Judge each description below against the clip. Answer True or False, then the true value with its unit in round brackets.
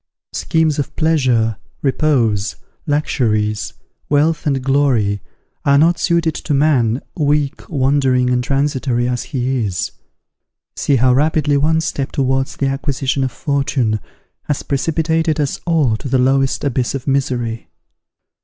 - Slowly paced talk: True (130 wpm)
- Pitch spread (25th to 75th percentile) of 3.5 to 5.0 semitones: False (2.9 semitones)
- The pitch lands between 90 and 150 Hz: True (135 Hz)